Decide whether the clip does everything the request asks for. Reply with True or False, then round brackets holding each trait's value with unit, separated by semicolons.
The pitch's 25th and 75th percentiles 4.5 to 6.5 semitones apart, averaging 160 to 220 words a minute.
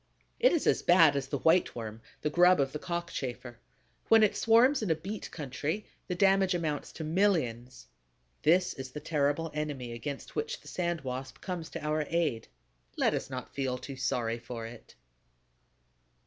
True (5.6 semitones; 175 wpm)